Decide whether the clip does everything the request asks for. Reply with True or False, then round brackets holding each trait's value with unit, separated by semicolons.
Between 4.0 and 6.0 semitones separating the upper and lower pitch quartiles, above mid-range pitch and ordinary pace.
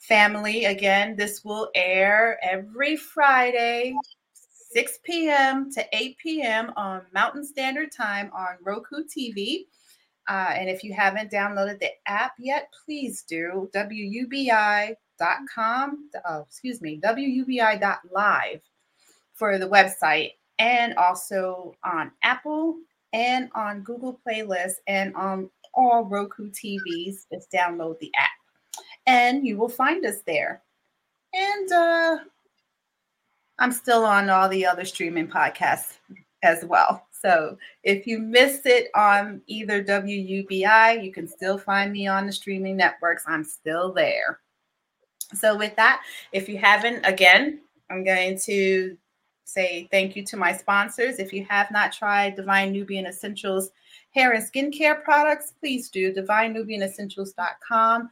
False (4.7 semitones; 210 Hz; 130 wpm)